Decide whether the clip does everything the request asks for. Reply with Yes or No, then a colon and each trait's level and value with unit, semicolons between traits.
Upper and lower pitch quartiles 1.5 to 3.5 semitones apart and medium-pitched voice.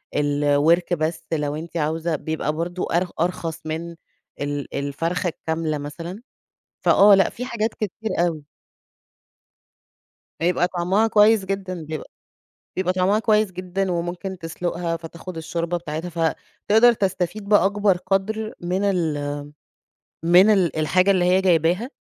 Yes: average, 3.1 semitones; medium, 175 Hz